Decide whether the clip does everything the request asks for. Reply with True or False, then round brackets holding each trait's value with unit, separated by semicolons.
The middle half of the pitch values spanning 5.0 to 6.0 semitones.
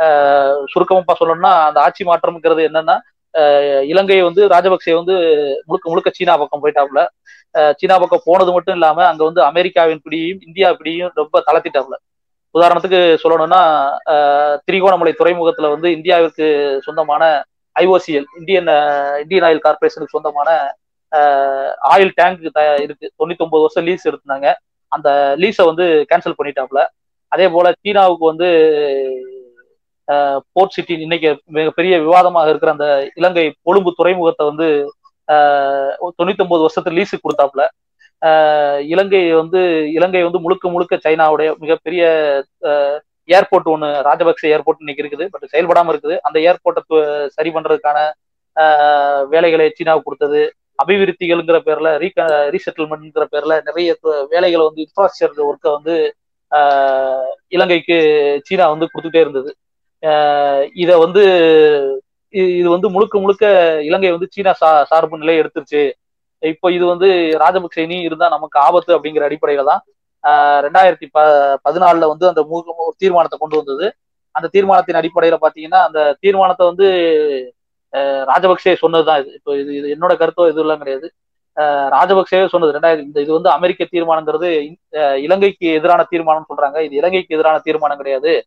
False (3.1 semitones)